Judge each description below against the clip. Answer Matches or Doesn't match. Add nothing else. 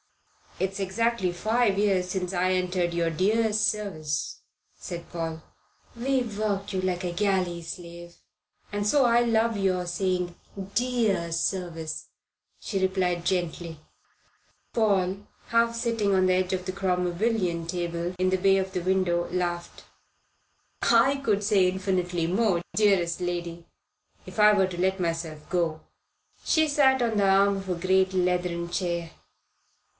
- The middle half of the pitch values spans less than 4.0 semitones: Matches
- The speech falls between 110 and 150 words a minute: Matches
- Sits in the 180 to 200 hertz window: Matches